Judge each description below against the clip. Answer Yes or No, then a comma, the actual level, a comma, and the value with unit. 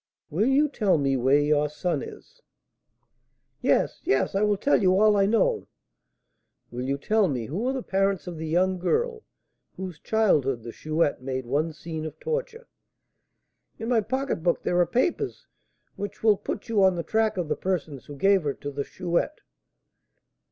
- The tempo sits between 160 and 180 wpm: Yes, average, 175 wpm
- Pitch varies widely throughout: Yes, wide, 6.6 semitones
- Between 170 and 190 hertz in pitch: Yes, medium, 185 Hz